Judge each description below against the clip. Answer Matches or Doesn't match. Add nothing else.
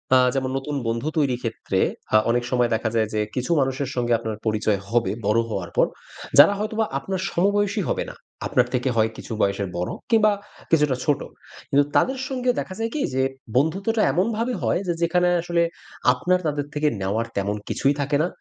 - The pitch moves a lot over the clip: Matches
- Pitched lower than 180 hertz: Matches